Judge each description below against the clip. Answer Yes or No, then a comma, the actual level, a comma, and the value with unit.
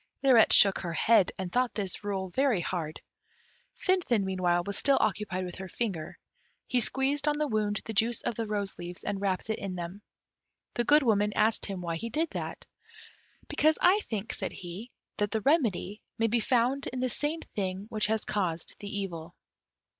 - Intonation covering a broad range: No, average, 4.4 semitones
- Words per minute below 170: No, average, 190 wpm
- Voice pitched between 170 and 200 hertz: No, high, 210 Hz